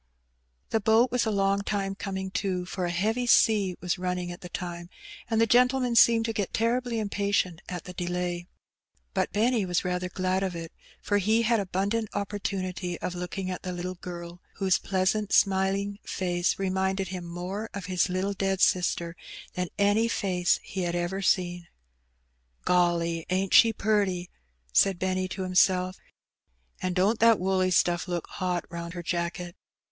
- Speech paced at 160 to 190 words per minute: Yes, average, 170 wpm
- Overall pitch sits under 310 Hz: Yes, medium, 185 Hz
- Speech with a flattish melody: Yes, narrow, 2.3 semitones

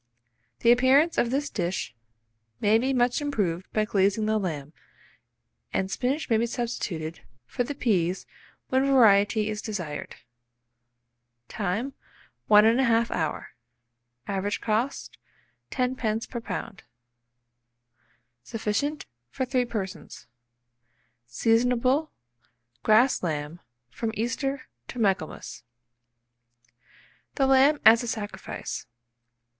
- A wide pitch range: No, average, 4.4 semitones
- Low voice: No, high, 225 Hz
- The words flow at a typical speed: No, slow, 100 wpm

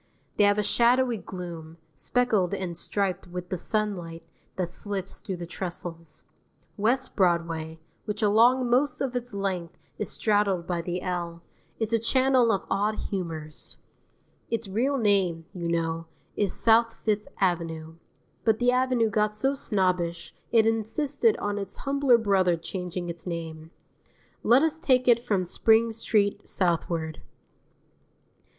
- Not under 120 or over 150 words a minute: Yes, average, 140 wpm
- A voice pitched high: Yes, high, 200 Hz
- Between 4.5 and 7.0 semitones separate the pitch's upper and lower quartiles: Yes, average, 5.0 semitones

